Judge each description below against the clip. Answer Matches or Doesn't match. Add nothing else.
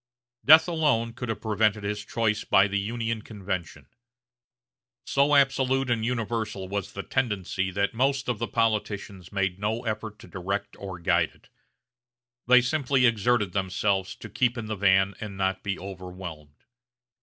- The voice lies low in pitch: Matches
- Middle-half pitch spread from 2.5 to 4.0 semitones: Matches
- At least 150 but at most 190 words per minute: Matches